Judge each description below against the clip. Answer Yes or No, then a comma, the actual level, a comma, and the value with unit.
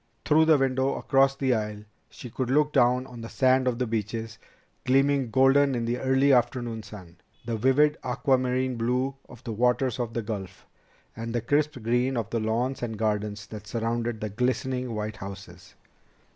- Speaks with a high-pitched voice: No, low, 120 Hz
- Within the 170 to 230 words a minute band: Yes, average, 175 wpm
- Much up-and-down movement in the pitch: No, average, 2.8 semitones